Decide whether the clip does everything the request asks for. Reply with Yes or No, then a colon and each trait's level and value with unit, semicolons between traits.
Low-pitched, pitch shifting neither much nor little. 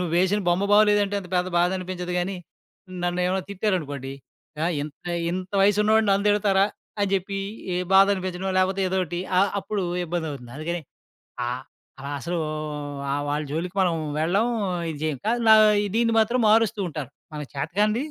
No: medium, 185 Hz; average, 3.0 semitones